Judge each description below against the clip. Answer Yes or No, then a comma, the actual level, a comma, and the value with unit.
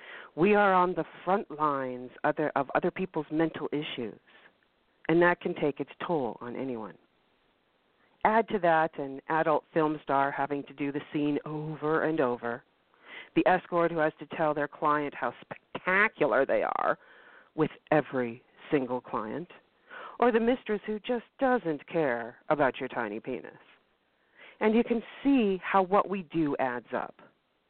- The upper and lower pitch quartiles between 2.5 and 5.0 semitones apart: No, wide, 5.6 semitones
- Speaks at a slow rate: No, average, 155 wpm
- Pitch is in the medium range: Yes, medium, 155 Hz